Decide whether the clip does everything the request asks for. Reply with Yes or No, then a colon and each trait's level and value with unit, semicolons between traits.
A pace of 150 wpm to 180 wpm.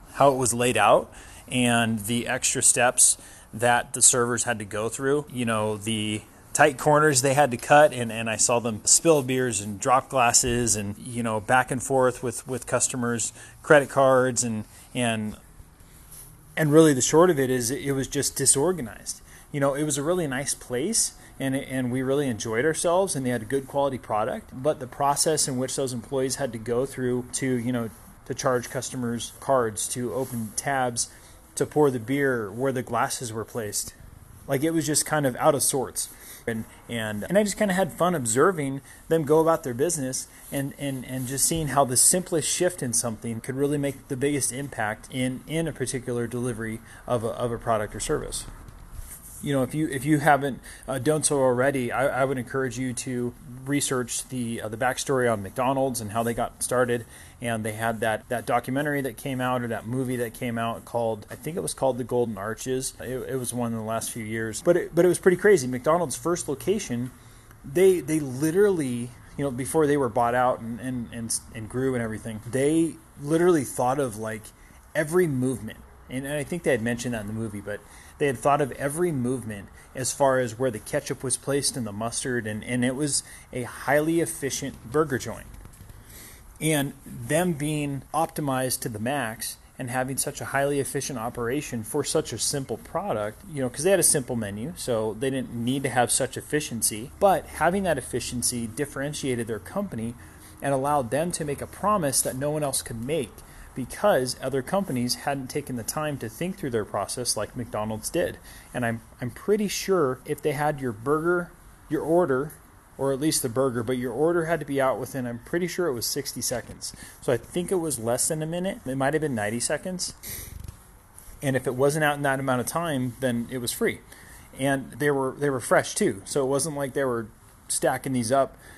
No: fast, 205 wpm